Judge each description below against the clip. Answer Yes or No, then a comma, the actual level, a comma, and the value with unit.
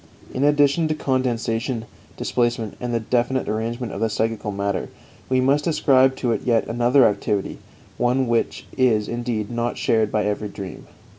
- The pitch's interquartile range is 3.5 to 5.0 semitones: No, average, 2.7 semitones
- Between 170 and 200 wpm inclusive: No, average, 155 wpm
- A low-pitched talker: Yes, low, 120 Hz